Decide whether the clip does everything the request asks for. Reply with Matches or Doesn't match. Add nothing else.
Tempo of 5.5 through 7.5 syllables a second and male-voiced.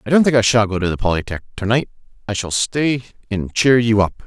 Matches